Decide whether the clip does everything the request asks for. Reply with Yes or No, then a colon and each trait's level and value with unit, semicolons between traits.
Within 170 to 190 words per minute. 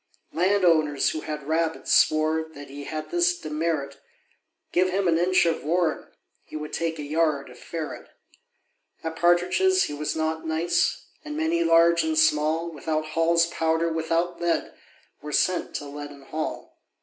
No: average, 160 wpm